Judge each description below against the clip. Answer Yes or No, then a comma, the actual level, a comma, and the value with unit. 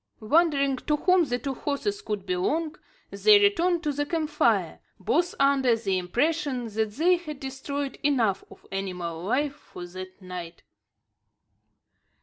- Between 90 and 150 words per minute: Yes, average, 140 wpm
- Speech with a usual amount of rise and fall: No, wide, 7.8 semitones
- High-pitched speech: Yes, very high, 275 Hz